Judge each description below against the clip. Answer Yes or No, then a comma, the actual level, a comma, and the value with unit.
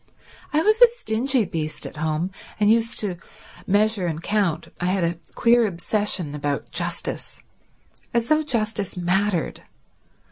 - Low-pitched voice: No, high, 205 Hz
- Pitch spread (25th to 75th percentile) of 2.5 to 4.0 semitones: No, average, 5.1 semitones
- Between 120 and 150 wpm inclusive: Yes, average, 140 wpm